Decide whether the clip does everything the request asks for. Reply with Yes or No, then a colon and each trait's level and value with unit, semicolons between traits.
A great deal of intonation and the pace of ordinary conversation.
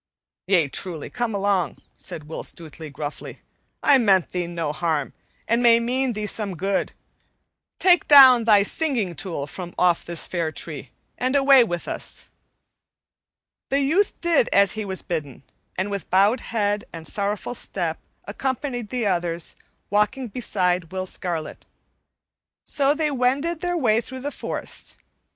Yes: wide, 6.6 semitones; average, 145 wpm